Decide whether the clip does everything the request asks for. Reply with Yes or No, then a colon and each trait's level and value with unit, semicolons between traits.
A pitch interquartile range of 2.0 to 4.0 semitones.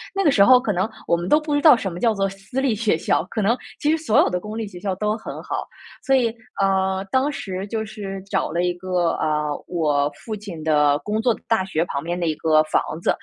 No: average, 4.7 semitones